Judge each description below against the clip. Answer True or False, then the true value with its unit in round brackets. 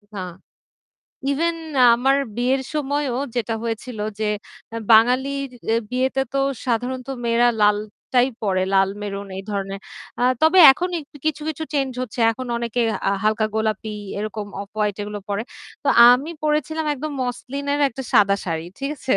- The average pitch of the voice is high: True (245 Hz)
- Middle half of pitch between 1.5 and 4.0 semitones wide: False (4.5 semitones)